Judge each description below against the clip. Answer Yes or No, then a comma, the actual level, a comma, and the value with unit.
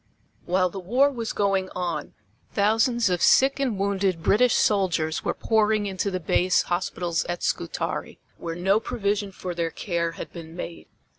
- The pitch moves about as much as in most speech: Yes, average, 3.3 semitones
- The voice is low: No, high, 190 Hz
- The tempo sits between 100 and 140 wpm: No, average, 160 wpm